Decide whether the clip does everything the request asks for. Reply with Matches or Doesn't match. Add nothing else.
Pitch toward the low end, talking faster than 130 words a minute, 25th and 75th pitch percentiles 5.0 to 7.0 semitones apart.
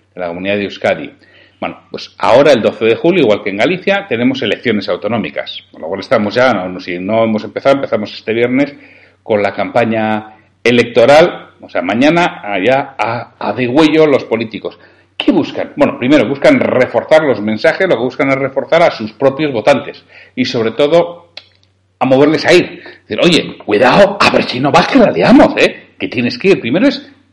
Matches